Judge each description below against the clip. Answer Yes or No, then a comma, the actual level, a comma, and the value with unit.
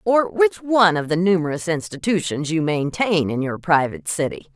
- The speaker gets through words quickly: No, average, 170 wpm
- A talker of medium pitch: Yes, medium, 175 Hz